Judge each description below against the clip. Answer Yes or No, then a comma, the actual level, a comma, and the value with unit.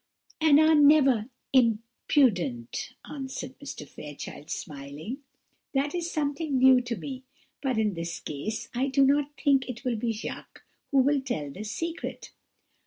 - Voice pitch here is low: No, very high, 255 Hz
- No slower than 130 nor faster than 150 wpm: Yes, average, 145 wpm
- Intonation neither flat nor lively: Yes, average, 5.0 semitones